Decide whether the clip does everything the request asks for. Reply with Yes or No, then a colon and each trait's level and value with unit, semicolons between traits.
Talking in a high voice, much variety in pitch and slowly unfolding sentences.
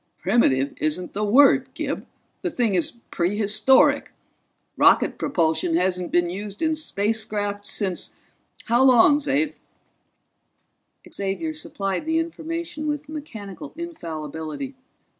Yes: high, 215 Hz; wide, 8.4 semitones; slow, 105 wpm